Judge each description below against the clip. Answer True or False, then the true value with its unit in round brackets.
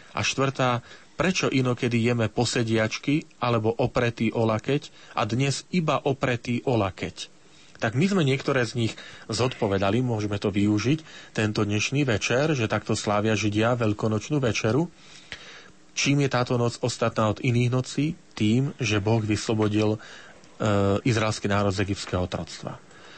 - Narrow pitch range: False (4.0 semitones)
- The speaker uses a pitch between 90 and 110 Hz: False (120 Hz)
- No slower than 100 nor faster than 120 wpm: False (135 wpm)